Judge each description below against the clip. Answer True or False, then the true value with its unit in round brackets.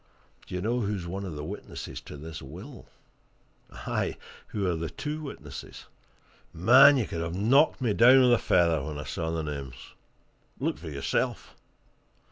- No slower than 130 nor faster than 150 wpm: False (170 wpm)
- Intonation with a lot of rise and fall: True (7.2 semitones)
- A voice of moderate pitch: False (90 Hz)